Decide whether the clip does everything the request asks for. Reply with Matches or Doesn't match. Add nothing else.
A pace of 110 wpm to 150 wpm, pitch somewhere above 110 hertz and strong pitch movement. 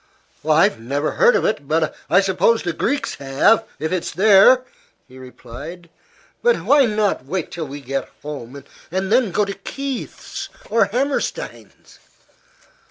Matches